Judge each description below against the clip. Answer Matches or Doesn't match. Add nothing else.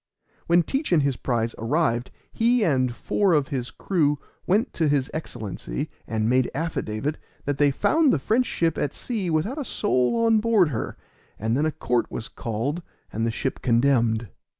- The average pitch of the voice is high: Doesn't match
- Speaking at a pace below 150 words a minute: Doesn't match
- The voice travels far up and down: Matches